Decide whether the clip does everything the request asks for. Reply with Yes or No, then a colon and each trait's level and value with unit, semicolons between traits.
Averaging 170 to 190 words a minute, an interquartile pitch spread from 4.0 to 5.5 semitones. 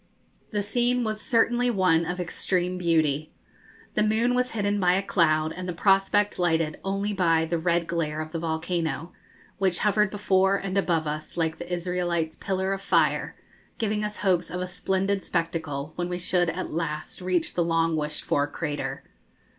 No: average, 175 wpm; average, 3.1 semitones